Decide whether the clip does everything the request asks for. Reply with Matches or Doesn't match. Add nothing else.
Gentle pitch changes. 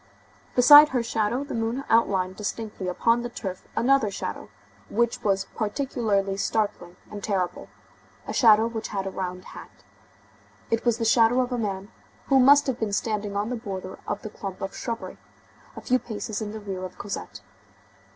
Doesn't match